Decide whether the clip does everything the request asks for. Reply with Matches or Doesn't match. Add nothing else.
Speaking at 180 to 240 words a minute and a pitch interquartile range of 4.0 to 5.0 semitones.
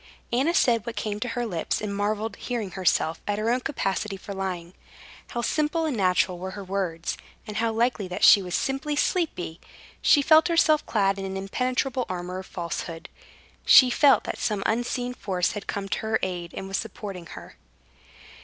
Matches